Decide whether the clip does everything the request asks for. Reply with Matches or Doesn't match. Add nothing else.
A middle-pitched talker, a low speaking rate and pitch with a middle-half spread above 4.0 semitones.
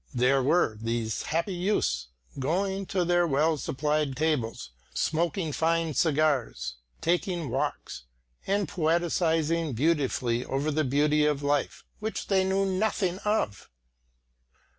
Matches